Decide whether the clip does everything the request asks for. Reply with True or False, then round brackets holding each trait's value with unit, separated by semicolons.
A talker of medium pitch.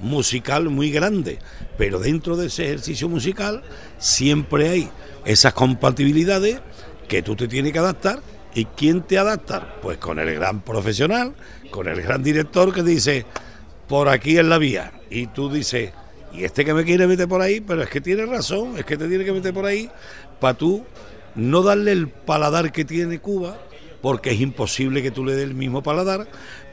True (150 Hz)